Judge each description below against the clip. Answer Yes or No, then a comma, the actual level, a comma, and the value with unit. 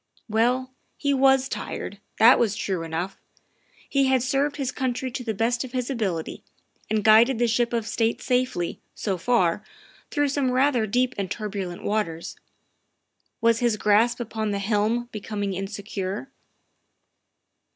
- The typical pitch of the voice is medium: No, high, 230 Hz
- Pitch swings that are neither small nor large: Yes, average, 3.9 semitones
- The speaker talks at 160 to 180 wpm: No, average, 145 wpm